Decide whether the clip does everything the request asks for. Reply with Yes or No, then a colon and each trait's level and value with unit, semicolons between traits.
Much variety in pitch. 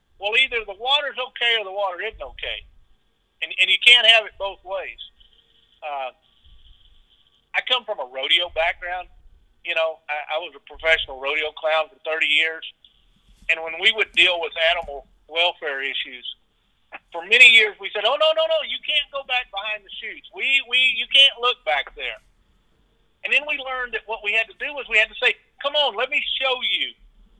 Yes: wide, 7.7 semitones